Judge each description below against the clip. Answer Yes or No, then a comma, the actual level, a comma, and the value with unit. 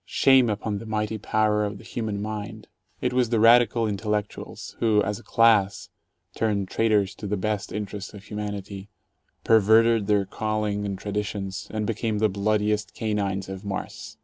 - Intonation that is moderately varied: No, narrow, 1.4 semitones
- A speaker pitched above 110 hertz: No, low, 105 Hz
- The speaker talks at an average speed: Yes, average, 165 wpm